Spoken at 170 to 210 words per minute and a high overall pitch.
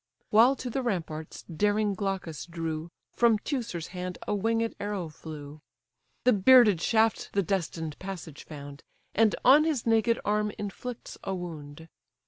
No: average, 140 wpm; high, 195 Hz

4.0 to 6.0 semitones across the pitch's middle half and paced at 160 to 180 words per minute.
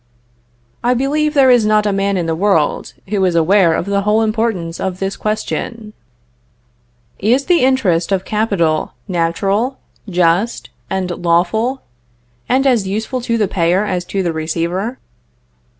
No: average, 4.6 semitones; average, 150 wpm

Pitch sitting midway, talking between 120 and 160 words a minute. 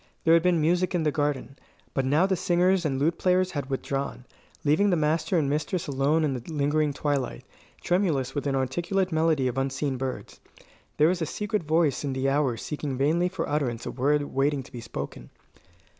No: medium, 150 Hz; average, 190 wpm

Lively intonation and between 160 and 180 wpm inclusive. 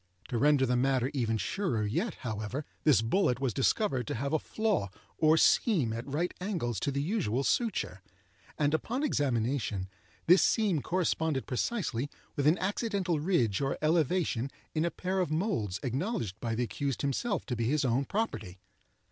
Yes: wide, 7.1 semitones; average, 165 wpm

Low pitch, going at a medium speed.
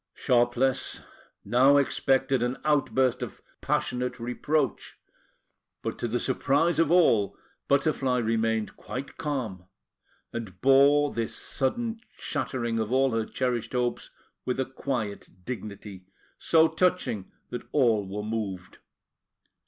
No: low, 125 Hz; slow, 115 wpm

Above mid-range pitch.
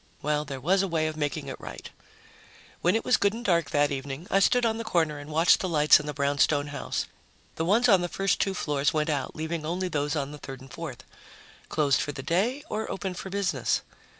No: medium, 155 Hz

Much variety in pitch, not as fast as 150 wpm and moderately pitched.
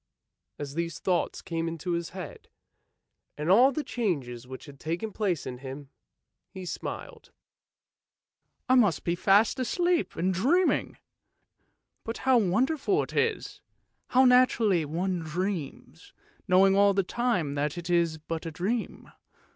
Yes: wide, 6.0 semitones; average, 140 wpm; medium, 180 Hz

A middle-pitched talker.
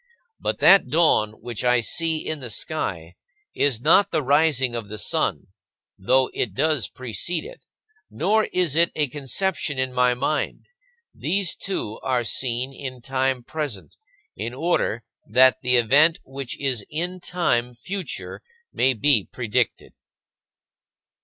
No: low, 130 Hz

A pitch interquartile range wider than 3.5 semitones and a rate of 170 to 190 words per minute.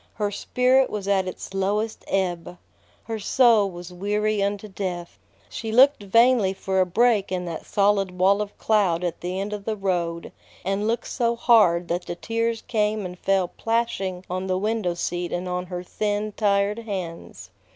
No: average, 3.0 semitones; average, 175 wpm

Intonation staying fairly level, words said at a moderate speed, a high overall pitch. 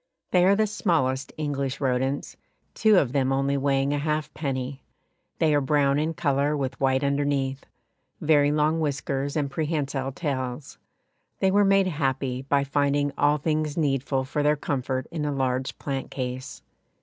No: narrow, 2.1 semitones; average, 155 wpm; medium, 140 Hz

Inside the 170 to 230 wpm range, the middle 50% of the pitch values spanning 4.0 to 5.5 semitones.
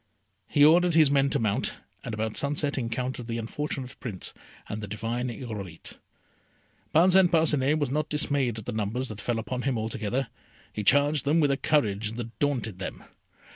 Yes: average, 175 wpm; average, 4.7 semitones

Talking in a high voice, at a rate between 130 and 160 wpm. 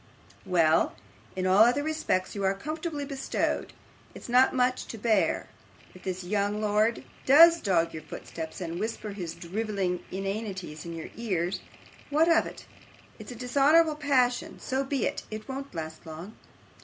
Yes: high, 215 Hz; average, 155 wpm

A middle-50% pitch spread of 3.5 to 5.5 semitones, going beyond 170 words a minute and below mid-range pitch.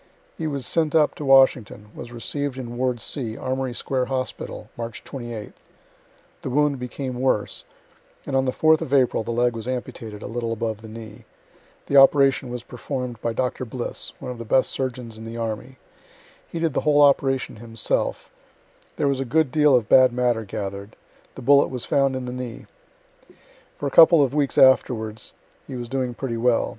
No: narrow, 2.6 semitones; average, 190 wpm; low, 125 Hz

